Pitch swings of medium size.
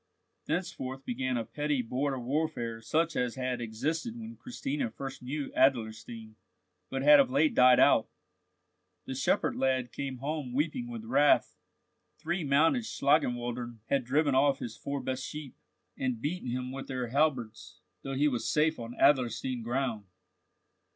Yes: average, 3.5 semitones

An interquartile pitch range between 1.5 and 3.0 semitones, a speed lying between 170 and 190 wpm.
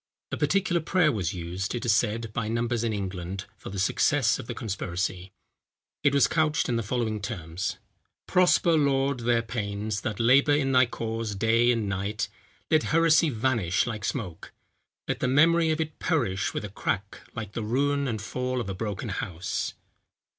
No: average, 5.3 semitones; average, 175 wpm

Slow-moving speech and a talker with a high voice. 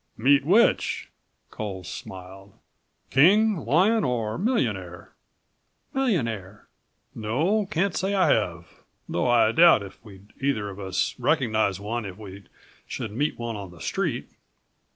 No: slow, 130 wpm; low, 115 Hz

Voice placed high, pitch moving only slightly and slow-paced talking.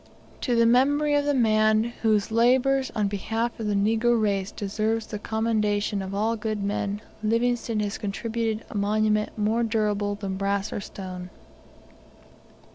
No: high, 215 Hz; narrow, 2.1 semitones; average, 150 wpm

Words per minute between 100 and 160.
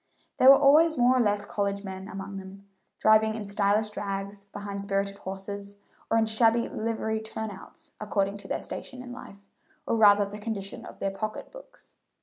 No: average, 180 wpm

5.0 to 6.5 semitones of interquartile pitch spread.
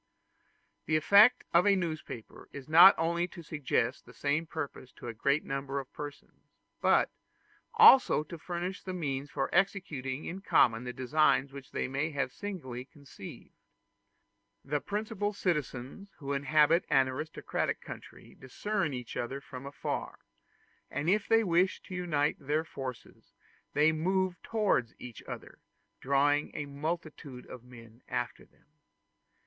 No: average, 4.6 semitones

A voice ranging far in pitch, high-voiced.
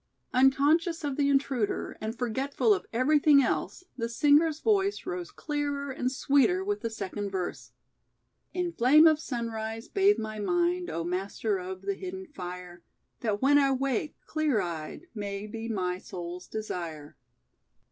Yes: wide, 6.9 semitones; very high, 255 Hz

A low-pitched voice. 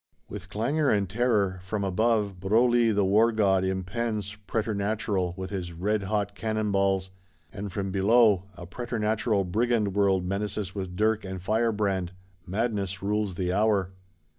Yes: low, 100 Hz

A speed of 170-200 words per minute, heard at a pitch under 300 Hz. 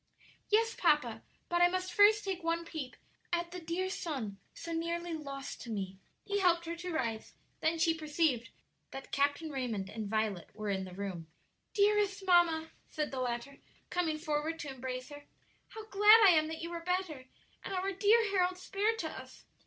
No: average, 185 wpm; very high, 330 Hz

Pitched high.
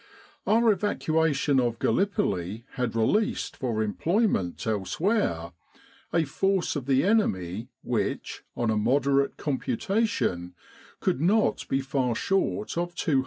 No: low, 135 Hz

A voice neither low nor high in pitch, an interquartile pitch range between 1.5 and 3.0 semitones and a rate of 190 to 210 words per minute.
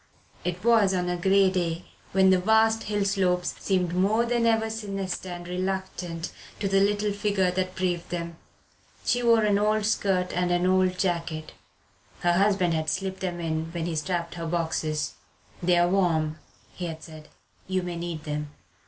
No: medium, 180 Hz; narrow, 2.4 semitones; average, 170 wpm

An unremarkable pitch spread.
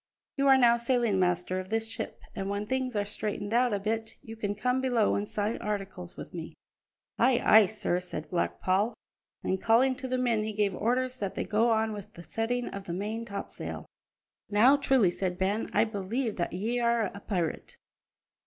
Yes: average, 3.2 semitones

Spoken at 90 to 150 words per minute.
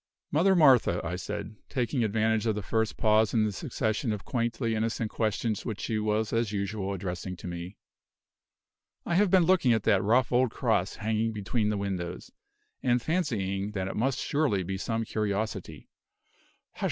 No: average, 175 wpm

